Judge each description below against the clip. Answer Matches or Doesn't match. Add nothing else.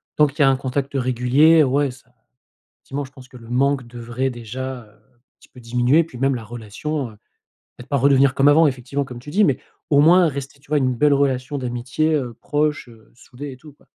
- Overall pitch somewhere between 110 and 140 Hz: Matches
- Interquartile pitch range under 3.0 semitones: Matches